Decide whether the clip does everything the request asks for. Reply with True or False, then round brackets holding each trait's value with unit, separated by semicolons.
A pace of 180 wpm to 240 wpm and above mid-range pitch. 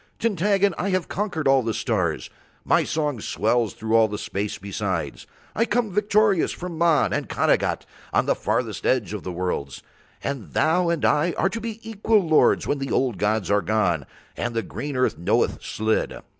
False (185 wpm; 135 Hz)